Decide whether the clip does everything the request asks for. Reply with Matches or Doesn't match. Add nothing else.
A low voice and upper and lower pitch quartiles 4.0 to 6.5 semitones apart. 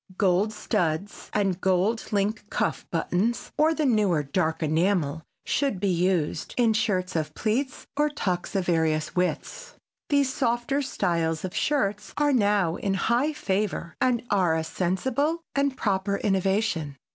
Doesn't match